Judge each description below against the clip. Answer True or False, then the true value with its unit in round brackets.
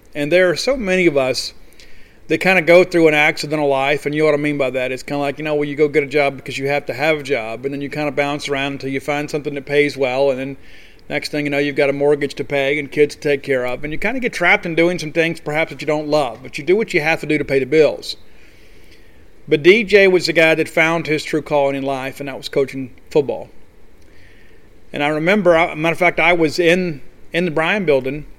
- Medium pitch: True (145 Hz)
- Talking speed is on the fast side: True (280 wpm)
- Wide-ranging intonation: False (2.9 semitones)